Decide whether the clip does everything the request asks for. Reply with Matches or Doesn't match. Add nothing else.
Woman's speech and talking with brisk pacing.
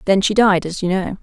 Matches